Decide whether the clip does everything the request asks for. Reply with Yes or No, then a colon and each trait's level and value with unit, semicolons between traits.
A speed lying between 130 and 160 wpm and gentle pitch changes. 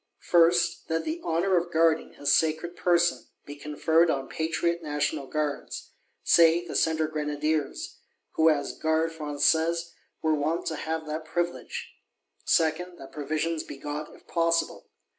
Yes: average, 140 wpm; narrow, 1.8 semitones